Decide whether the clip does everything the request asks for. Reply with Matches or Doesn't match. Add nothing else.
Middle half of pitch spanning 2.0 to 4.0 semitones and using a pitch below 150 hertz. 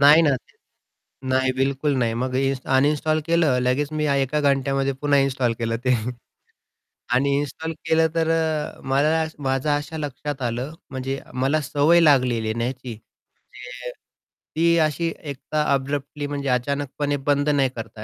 Matches